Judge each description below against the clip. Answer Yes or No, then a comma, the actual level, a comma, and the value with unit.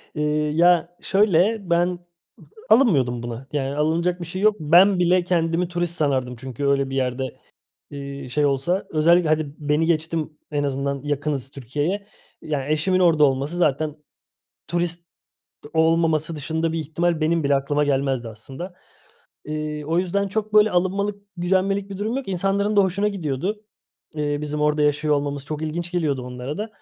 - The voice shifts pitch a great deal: No, average, 3.8 semitones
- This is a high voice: No, medium, 155 Hz